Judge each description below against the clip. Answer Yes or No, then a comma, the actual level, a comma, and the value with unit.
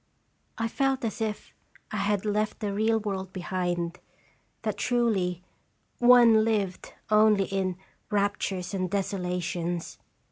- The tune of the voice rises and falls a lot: No, average, 3.0 semitones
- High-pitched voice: Yes, high, 200 Hz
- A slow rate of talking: Yes, slow, 120 wpm